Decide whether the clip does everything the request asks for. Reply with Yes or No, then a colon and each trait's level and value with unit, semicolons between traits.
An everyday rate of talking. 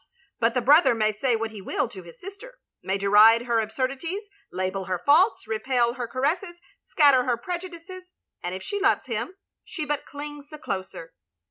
Yes: average, 175 wpm